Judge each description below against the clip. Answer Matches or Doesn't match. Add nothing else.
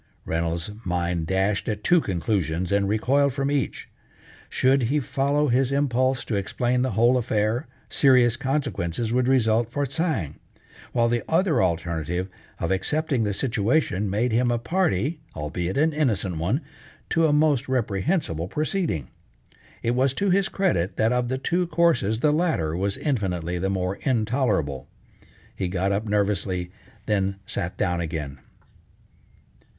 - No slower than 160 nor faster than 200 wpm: Doesn't match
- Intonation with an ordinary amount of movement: Doesn't match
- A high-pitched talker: Doesn't match